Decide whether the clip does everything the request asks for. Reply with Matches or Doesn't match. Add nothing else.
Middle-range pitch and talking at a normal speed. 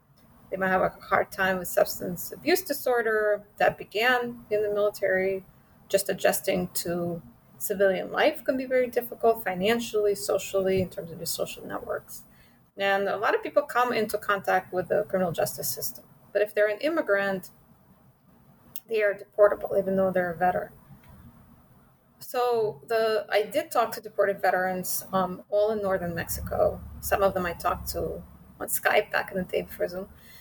Doesn't match